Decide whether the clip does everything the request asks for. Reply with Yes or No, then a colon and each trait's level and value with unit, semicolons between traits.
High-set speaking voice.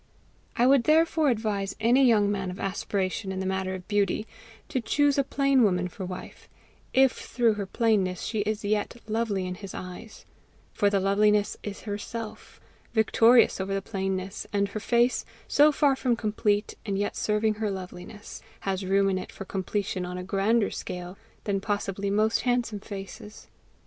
Yes: high, 205 Hz